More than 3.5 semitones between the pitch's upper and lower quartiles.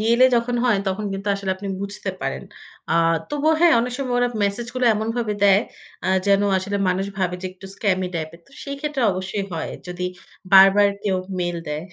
Yes: average, 3.9 semitones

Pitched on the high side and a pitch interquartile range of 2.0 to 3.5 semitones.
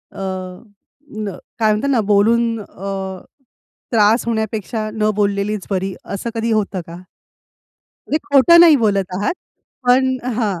Yes: high, 210 Hz; average, 2.9 semitones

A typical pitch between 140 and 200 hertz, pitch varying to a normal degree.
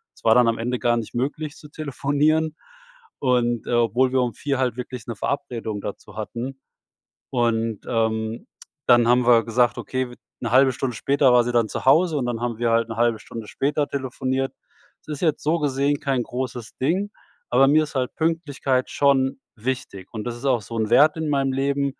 No: low, 125 Hz; average, 3.1 semitones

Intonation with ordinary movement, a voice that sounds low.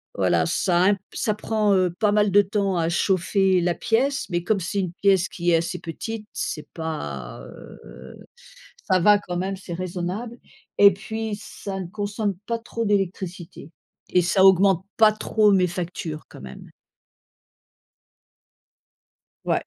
No: average, 3.1 semitones; high, 190 Hz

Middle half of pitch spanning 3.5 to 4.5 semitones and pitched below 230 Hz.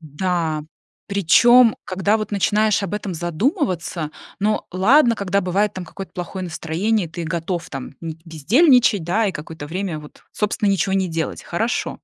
Yes: average, 4.2 semitones; medium, 185 Hz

